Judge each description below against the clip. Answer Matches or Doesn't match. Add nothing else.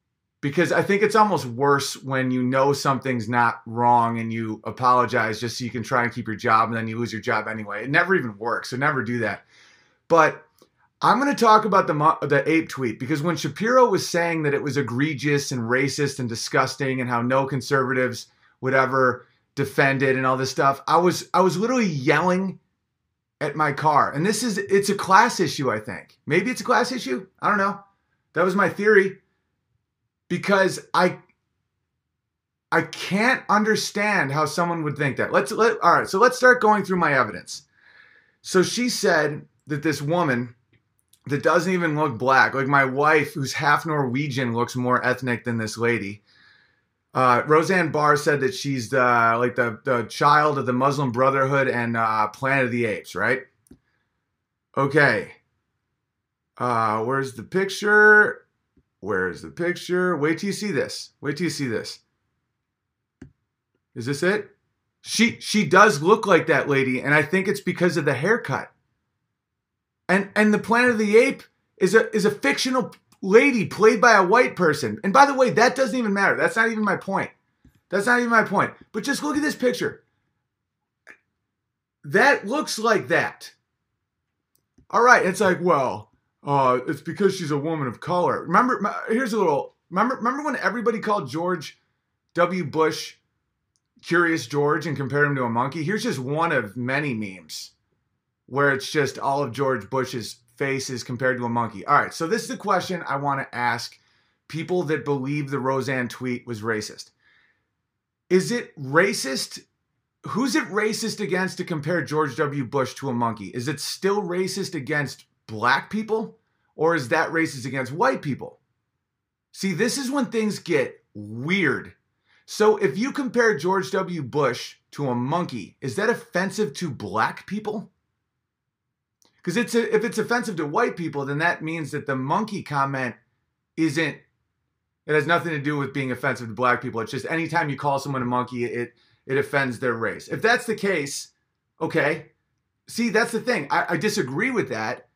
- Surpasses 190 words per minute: Doesn't match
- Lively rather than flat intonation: Matches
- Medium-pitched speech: Matches